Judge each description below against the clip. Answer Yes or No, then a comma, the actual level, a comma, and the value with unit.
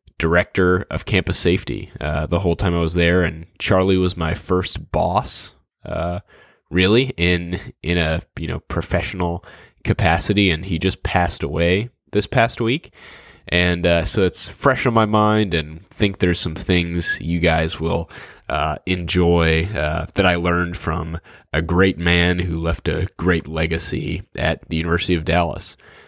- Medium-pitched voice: No, very low, 85 Hz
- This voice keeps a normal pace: Yes, average, 160 wpm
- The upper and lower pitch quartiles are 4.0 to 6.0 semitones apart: No, narrow, 2.4 semitones